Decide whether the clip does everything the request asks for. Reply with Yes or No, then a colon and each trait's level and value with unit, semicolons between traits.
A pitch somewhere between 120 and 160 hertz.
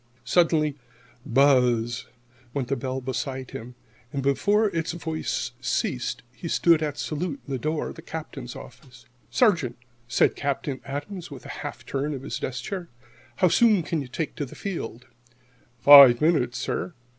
Yes: medium, 140 Hz